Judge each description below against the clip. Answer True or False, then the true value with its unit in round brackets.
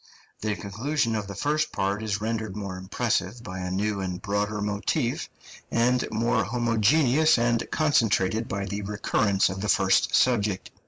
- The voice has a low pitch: True (105 Hz)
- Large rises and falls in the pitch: False (3.0 semitones)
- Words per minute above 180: False (155 wpm)